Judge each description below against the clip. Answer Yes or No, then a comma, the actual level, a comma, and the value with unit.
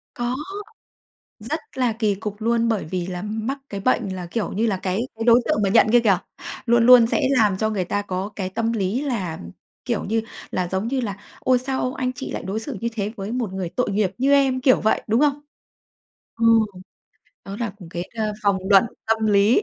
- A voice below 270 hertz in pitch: Yes, high, 220 Hz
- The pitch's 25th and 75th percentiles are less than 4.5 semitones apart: Yes, average, 3.7 semitones